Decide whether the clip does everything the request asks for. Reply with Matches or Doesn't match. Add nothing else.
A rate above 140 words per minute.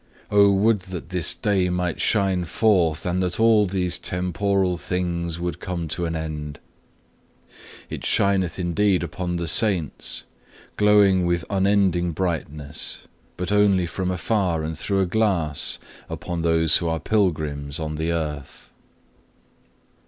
Doesn't match